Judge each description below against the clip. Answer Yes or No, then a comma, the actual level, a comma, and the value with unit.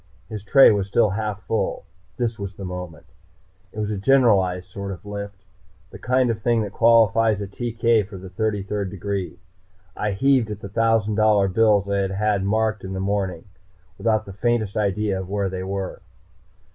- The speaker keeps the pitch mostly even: Yes, narrow, 2.3 semitones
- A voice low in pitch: Yes, low, 100 Hz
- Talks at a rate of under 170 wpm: No, average, 185 wpm